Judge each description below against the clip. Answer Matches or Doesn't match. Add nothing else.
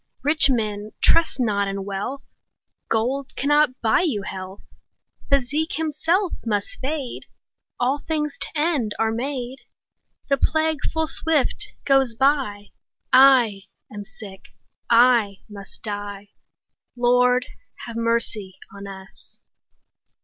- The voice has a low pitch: Doesn't match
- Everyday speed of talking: Doesn't match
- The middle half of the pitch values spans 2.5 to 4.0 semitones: Doesn't match